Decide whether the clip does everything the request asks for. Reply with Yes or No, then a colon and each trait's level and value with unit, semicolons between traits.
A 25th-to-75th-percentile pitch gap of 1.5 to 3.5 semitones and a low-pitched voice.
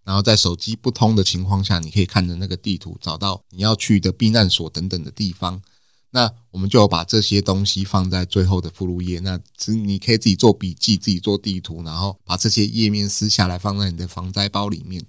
Yes: narrow, 2.6 semitones; low, 100 Hz